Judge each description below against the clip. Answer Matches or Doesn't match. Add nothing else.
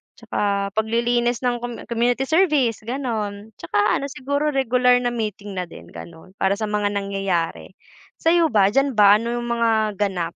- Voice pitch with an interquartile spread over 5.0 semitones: Doesn't match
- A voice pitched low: Doesn't match